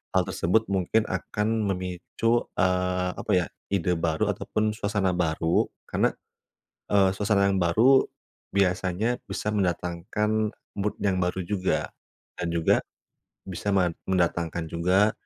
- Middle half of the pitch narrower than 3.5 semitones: Yes, average, 2.8 semitones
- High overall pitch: No, very low, 95 Hz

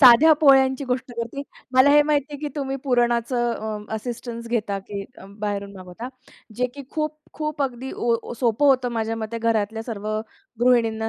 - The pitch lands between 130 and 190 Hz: No, high, 240 Hz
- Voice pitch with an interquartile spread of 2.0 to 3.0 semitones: No, average, 3.4 semitones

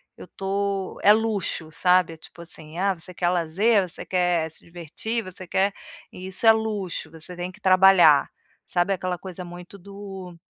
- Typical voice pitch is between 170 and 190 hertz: Yes, medium, 185 Hz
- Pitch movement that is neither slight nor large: No, narrow, 2.3 semitones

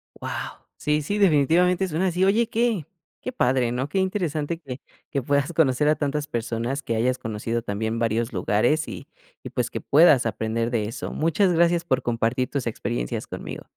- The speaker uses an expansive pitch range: Yes, wide, 6.4 semitones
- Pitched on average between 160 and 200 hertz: No, medium, 140 Hz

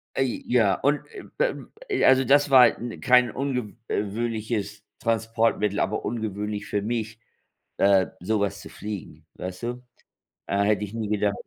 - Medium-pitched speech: No, low, 110 Hz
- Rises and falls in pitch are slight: No, average, 3.1 semitones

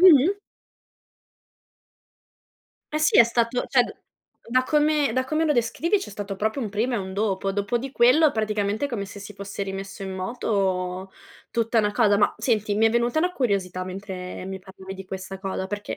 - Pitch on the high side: Yes, high, 210 Hz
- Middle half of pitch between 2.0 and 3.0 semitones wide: No, average, 4.3 semitones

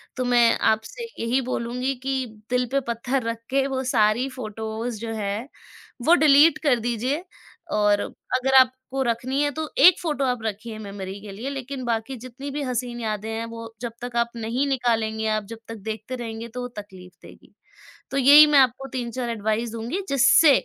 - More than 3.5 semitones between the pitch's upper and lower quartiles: No, average, 3.2 semitones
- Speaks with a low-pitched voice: No, high, 240 Hz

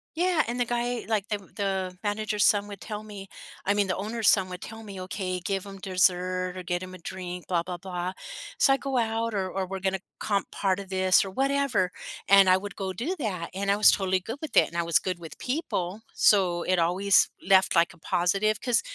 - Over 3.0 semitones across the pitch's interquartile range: No, average, 2.7 semitones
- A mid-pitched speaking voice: No, high, 195 Hz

